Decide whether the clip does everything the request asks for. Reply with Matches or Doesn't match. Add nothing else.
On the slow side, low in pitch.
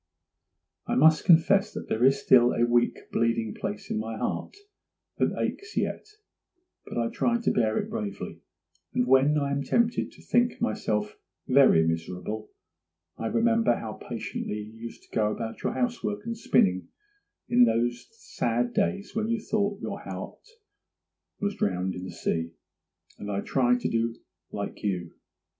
Doesn't match